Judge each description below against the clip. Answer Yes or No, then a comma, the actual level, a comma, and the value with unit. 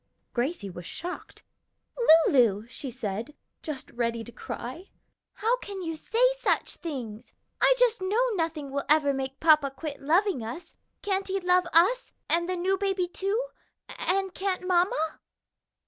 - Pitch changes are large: Yes, wide, 6.3 semitones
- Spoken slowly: No, average, 145 wpm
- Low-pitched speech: No, very high, 335 Hz